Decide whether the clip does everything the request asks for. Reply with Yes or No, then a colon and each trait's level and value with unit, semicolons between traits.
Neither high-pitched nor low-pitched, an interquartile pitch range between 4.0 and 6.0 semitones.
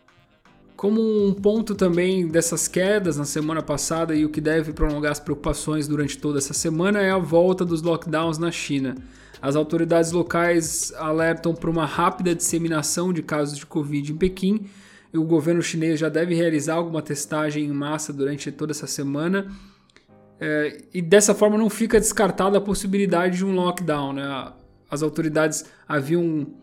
No: medium, 165 Hz; average, 3.1 semitones